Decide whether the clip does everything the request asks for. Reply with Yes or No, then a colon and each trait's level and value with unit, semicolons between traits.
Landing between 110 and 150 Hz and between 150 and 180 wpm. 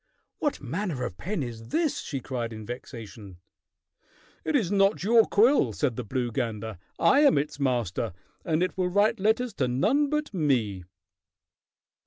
Yes: medium, 140 Hz; average, 160 wpm